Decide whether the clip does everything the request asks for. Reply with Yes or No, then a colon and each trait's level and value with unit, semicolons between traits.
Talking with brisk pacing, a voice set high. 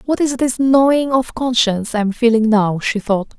Yes: fast, 215 wpm; high, 235 Hz